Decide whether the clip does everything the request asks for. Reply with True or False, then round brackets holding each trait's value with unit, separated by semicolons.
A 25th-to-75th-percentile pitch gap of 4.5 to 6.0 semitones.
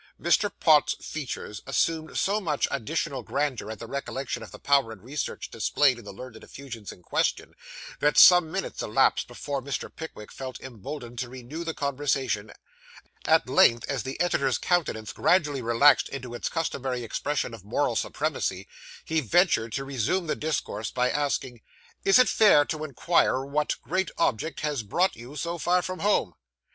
True (5.0 semitones)